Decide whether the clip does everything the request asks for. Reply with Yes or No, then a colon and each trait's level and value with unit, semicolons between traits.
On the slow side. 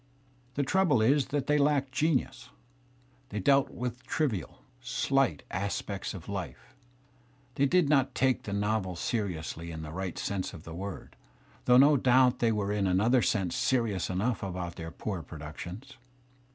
No: average, 165 wpm